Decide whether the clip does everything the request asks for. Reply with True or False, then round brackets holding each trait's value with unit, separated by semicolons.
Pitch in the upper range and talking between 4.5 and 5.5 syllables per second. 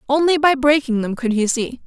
True (265 Hz; 5.4 syllables/s)